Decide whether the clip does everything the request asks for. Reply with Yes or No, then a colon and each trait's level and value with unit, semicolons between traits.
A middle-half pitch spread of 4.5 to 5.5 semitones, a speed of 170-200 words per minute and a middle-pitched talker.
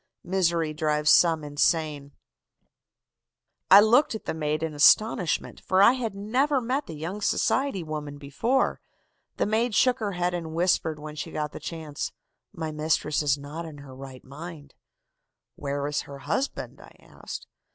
No: average, 5.2 semitones; average, 160 wpm; medium, 160 Hz